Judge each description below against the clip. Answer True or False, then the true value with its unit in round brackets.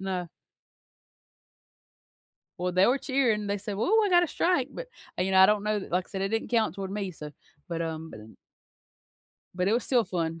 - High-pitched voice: True (195 Hz)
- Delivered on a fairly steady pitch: False (4.4 semitones)